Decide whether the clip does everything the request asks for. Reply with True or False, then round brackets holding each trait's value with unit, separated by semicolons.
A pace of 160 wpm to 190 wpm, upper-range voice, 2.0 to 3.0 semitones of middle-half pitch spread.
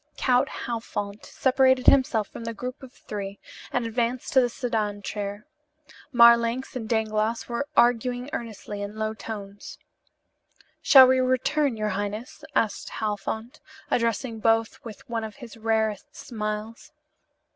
False (135 wpm; 230 Hz; 2.6 semitones)